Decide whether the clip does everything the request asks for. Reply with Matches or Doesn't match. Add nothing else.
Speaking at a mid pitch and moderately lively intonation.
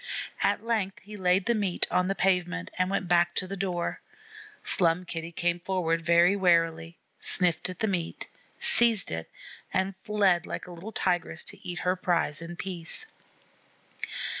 Doesn't match